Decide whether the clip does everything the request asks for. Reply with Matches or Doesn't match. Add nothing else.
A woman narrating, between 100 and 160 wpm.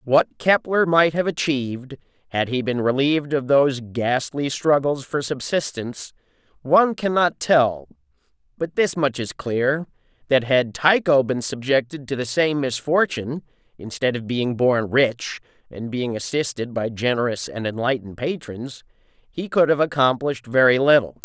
Doesn't match